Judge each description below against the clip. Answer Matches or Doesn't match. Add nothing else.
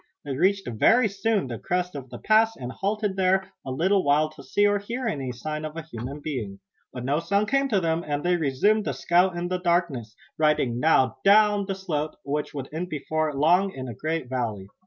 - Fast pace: Matches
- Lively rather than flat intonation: Matches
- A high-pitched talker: Doesn't match